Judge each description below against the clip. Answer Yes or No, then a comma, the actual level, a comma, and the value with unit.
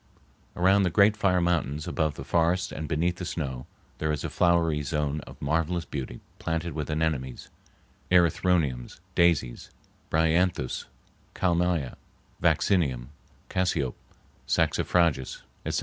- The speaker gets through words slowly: Yes, slow, 120 wpm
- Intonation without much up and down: No, average, 3.4 semitones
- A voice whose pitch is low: Yes, very low, 80 Hz